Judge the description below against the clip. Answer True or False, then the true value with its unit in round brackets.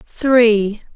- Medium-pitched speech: False (225 Hz)